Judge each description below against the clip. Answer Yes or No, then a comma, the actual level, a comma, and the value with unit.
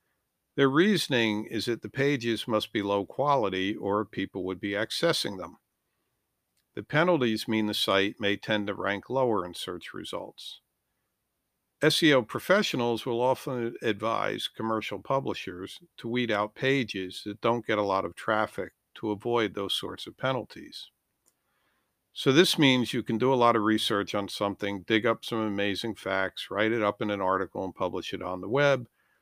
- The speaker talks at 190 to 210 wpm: No, average, 170 wpm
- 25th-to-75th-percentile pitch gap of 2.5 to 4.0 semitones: Yes, average, 3.0 semitones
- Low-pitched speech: Yes, low, 110 Hz